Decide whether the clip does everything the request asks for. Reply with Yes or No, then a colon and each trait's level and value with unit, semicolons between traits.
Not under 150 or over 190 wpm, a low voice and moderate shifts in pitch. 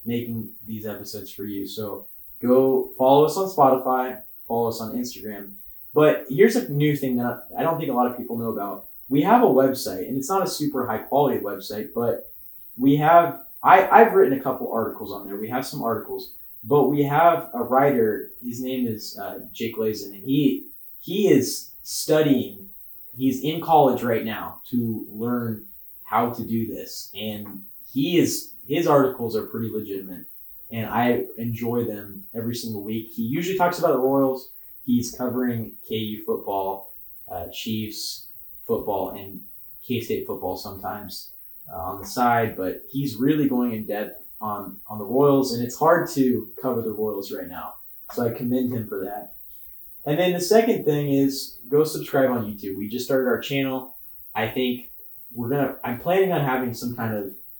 Yes: average, 180 wpm; low, 125 Hz; average, 4.2 semitones